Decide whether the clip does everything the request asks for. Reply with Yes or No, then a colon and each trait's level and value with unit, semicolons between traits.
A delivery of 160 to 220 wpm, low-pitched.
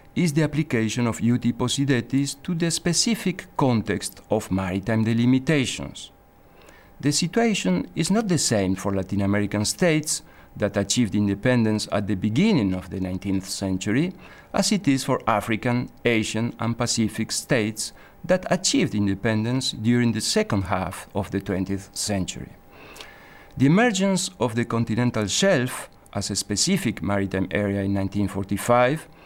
No: slow, 135 wpm; low, 115 Hz